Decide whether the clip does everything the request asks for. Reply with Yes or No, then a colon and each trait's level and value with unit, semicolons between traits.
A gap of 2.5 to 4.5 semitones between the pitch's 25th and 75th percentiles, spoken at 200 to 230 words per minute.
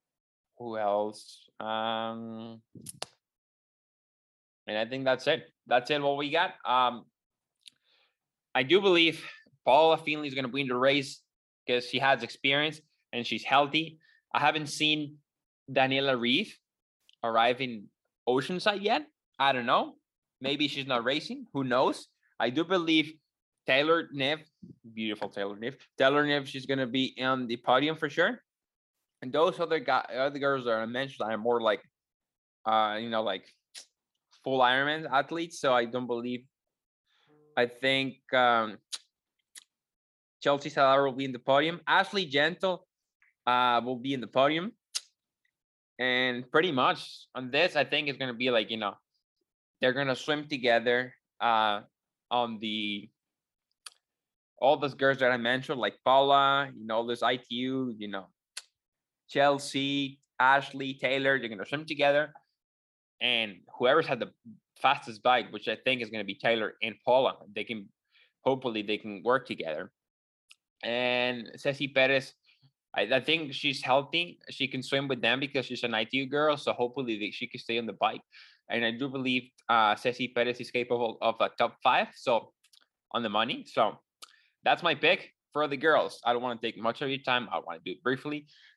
No: average, 3.5 semitones; average, 165 wpm